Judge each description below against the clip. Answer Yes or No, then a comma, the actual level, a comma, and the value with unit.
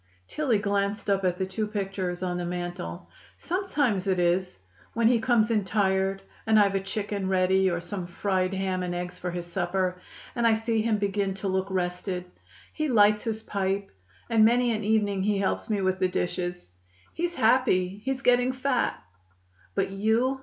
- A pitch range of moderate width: Yes, average, 3.2 semitones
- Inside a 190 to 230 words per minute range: No, average, 180 wpm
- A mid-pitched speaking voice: No, high, 195 Hz